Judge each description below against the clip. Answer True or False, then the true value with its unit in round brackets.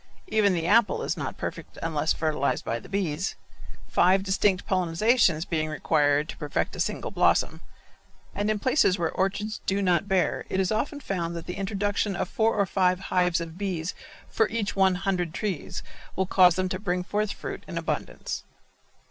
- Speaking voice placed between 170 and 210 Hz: True (185 Hz)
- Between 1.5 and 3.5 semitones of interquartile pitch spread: True (3.2 semitones)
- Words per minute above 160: True (180 wpm)